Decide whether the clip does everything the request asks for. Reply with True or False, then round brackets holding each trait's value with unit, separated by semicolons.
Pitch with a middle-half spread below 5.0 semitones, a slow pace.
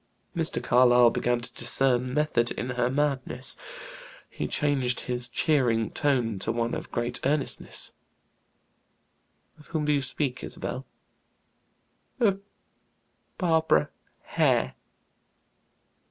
True (3.3 semitones; 105 wpm)